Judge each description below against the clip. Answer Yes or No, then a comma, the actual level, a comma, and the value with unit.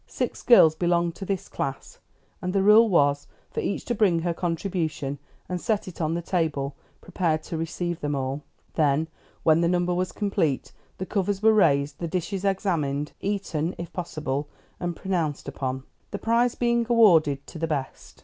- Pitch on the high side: No, medium, 170 Hz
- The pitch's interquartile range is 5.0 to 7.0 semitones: No, average, 4.4 semitones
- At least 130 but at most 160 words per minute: No, average, 175 wpm